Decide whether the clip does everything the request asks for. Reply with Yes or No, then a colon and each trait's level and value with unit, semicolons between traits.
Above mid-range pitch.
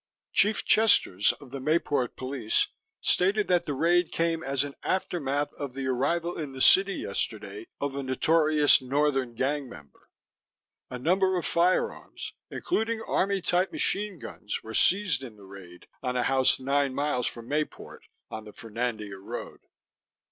No: medium, 140 Hz